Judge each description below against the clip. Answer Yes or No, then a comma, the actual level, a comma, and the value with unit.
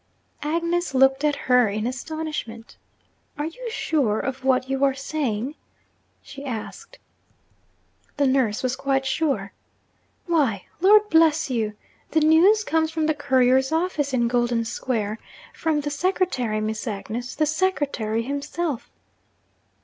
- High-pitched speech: Yes, very high, 275 Hz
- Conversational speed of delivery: No, slow, 130 wpm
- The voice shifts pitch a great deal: No, average, 4.8 semitones